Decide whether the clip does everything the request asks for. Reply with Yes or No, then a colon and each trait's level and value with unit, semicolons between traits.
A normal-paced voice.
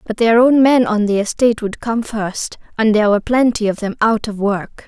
No: fast, 235 wpm